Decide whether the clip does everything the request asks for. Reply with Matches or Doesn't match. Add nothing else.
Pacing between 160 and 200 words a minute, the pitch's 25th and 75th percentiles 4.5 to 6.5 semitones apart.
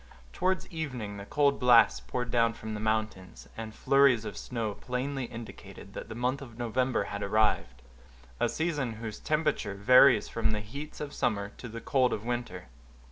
Doesn't match